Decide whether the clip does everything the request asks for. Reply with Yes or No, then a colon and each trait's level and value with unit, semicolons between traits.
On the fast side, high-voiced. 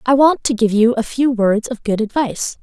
Yes: fast, 250 wpm; high, 240 Hz